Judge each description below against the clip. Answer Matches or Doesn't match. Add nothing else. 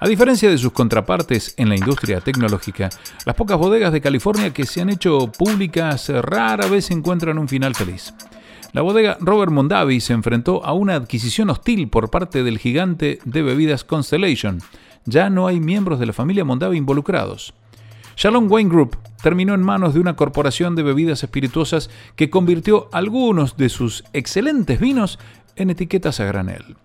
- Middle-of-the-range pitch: Matches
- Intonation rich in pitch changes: Matches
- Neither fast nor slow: Matches